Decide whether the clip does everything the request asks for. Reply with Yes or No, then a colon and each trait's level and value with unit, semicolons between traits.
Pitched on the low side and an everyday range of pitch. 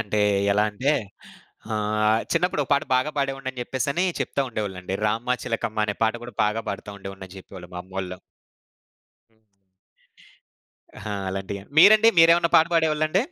No: low, 110 Hz; wide, 5.9 semitones